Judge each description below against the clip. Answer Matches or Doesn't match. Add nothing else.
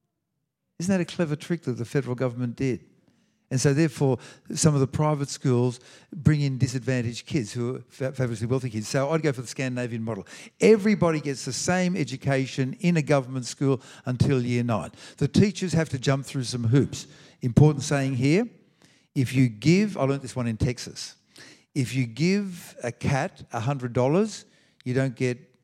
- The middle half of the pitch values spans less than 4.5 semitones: Matches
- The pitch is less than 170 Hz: Matches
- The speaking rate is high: Doesn't match